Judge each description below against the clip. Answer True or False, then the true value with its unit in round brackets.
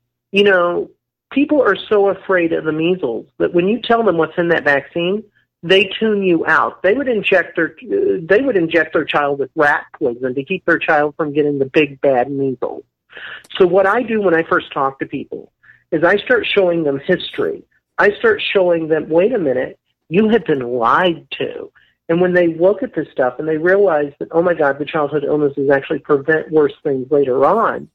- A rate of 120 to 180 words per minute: False (205 wpm)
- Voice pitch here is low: False (170 Hz)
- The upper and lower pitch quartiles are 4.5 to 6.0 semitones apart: True (5.1 semitones)